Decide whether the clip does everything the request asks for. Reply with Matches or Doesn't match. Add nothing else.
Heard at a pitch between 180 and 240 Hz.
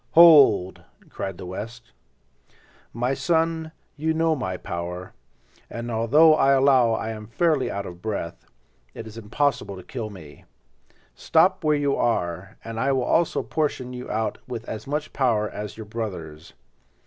Doesn't match